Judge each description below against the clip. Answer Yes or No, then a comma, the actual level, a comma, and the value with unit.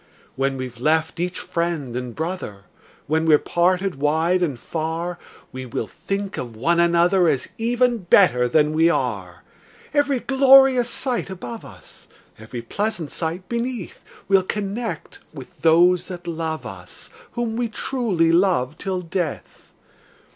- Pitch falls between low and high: Yes, medium, 170 Hz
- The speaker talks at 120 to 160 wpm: Yes, average, 140 wpm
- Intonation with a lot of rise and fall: No, average, 4.5 semitones